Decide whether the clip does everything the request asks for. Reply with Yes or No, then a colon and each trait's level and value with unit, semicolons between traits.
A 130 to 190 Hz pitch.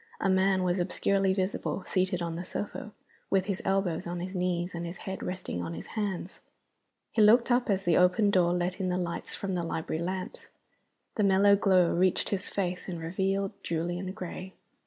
Yes: medium, 185 Hz